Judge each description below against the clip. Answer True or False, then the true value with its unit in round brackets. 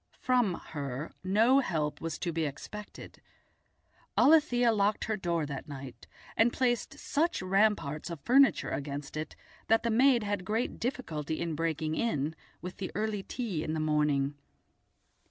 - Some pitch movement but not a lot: False (6.9 semitones)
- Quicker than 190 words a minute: False (150 wpm)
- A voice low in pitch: False (185 Hz)